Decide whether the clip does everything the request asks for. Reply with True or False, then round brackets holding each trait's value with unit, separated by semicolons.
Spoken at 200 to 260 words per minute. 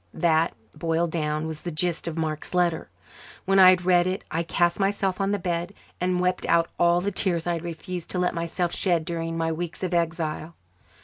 True (205 wpm)